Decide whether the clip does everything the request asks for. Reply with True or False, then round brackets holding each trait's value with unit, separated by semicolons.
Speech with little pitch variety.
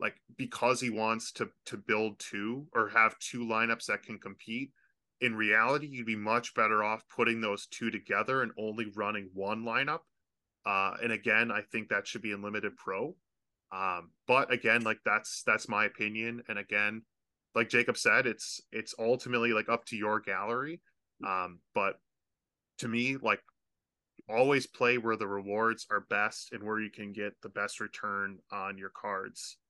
True (2.1 semitones)